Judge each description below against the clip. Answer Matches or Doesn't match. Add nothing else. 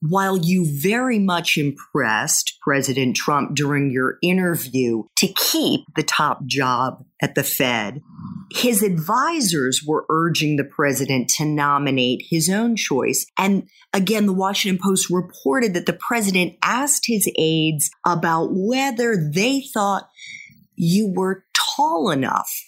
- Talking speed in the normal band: Doesn't match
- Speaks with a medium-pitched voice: Matches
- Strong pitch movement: Matches